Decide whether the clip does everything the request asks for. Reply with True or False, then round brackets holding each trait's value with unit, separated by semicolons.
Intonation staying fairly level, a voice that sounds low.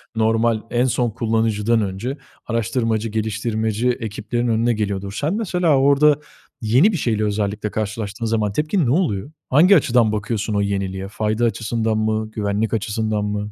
True (2.3 semitones; 110 Hz)